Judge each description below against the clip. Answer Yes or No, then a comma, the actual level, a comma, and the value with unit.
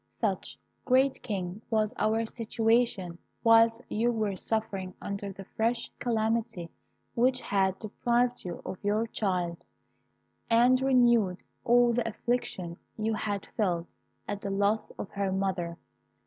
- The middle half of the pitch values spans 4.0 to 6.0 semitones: No, average, 3.4 semitones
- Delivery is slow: Yes, slow, 130 wpm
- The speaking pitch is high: Yes, high, 220 Hz